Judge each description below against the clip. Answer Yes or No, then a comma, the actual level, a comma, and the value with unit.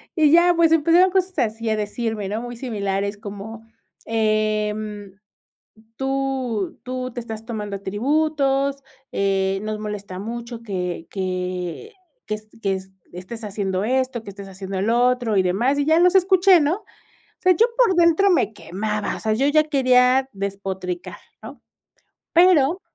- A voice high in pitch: Yes, high, 225 Hz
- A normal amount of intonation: No, wide, 5.7 semitones